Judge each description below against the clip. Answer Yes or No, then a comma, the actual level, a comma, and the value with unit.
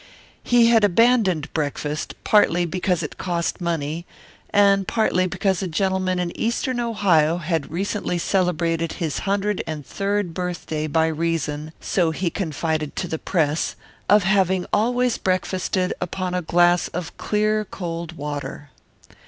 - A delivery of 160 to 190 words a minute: No, slow, 135 wpm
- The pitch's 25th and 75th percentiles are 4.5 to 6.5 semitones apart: No, average, 3.4 semitones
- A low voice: No, medium, 180 Hz